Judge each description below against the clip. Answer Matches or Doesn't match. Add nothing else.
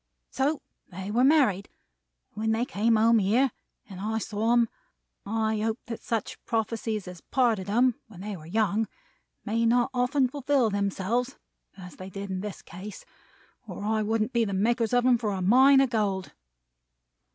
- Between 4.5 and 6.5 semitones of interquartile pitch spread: Doesn't match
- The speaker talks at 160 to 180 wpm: Matches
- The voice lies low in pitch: Doesn't match